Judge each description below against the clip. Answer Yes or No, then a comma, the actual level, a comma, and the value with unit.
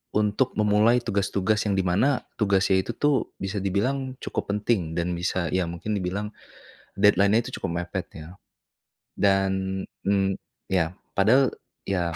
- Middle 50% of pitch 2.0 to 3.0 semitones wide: Yes, narrow, 2.5 semitones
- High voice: No, low, 100 Hz